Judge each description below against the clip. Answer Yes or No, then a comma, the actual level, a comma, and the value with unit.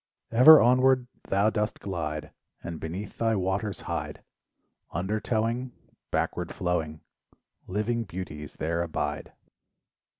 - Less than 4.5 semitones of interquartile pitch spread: No, average, 5.3 semitones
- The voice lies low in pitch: Yes, low, 100 Hz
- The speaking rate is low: Yes, slow, 100 wpm